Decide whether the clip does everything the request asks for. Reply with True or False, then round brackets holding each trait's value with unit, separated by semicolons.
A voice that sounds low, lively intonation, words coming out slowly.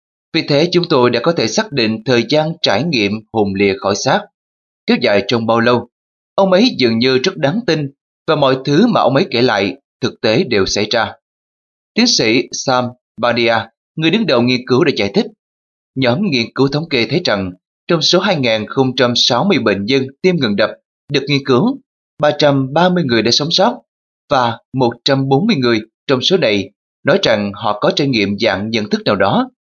False (130 Hz; 6.0 semitones; 190 wpm)